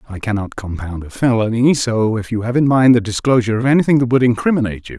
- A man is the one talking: Yes, male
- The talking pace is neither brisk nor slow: No, fast, 240 wpm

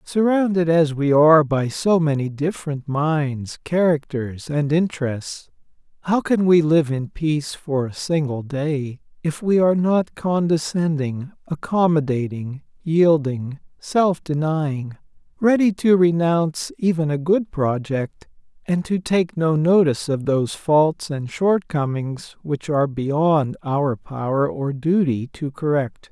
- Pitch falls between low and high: Yes, medium, 155 Hz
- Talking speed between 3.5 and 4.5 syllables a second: Yes, 4.0 syllables/s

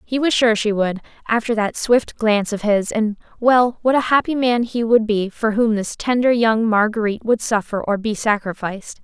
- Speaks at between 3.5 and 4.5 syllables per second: No, 5.0 syllables/s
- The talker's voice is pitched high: Yes, high, 220 Hz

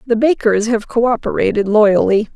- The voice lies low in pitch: No, high, 225 Hz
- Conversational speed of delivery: Yes, average, 155 wpm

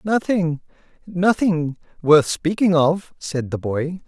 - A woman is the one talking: No, male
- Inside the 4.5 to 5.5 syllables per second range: No, 3.4 syllables/s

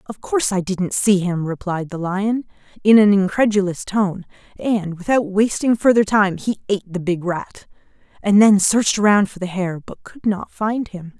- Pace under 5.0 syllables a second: Yes, 4.8 syllables/s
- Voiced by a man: No, female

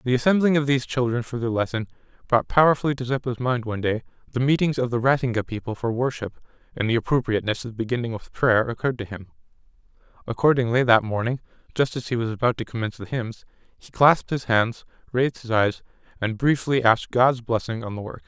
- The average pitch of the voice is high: No, low, 120 Hz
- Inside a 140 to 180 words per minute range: No, average, 195 wpm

